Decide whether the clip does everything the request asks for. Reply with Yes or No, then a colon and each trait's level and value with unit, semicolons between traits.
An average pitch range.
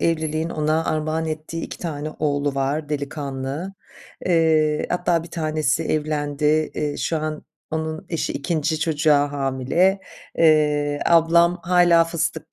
No: narrow, 2.0 semitones